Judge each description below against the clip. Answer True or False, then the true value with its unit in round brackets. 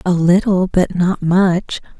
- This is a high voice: False (180 Hz)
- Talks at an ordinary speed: True (150 wpm)